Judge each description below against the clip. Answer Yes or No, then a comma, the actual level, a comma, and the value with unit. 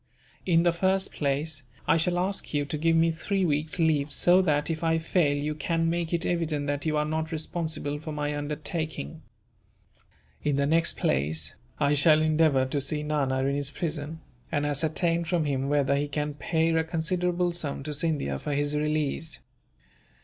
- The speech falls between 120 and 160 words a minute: No, average, 180 wpm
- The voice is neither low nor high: Yes, medium, 155 Hz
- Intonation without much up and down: Yes, narrow, 2.3 semitones